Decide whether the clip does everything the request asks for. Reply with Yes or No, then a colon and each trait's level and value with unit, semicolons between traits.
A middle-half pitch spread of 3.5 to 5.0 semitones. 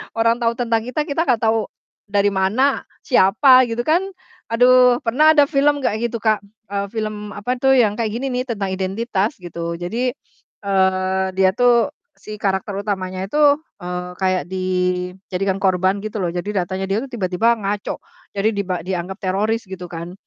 Yes: average, 3.9 semitones